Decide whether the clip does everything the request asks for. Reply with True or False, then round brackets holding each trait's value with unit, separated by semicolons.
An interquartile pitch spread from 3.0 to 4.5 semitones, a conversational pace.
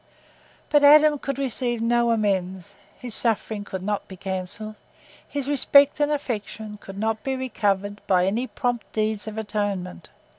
True (4.1 semitones; 150 wpm)